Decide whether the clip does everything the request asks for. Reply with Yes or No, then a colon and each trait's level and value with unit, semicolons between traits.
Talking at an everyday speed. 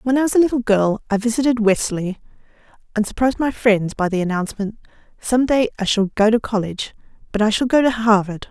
Yes: average, 195 wpm